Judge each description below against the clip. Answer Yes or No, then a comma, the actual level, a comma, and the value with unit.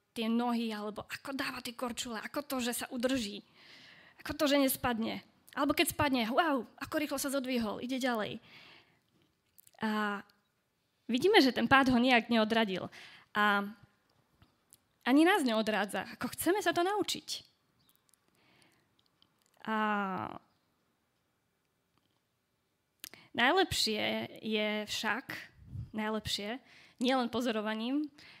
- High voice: Yes, high, 245 Hz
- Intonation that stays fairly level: No, average, 4.4 semitones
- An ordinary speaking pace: No, slow, 105 wpm